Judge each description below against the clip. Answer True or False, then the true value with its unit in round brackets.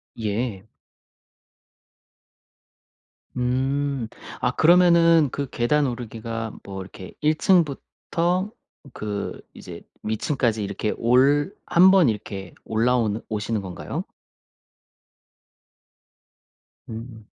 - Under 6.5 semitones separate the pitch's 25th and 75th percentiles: True (5.4 semitones)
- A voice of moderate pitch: False (120 Hz)